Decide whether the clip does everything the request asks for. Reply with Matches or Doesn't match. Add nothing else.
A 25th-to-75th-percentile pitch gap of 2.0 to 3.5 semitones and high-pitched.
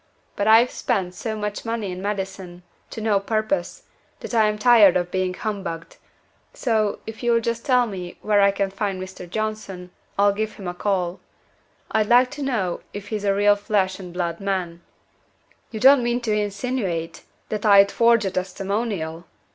Matches